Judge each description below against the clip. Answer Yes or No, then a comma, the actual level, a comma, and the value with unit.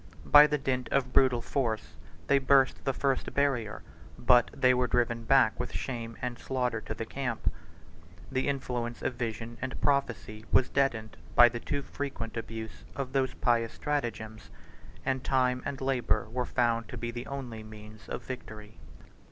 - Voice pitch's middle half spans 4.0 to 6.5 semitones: No, average, 2.7 semitones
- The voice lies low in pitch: Yes, low, 125 Hz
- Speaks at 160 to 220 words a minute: Yes, average, 165 wpm